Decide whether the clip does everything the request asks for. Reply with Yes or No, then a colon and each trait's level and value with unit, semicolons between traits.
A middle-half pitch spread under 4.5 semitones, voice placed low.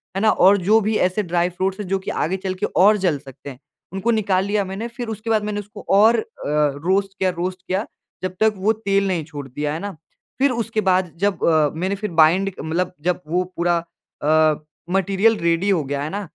No: average, 3.2 semitones; high, 190 Hz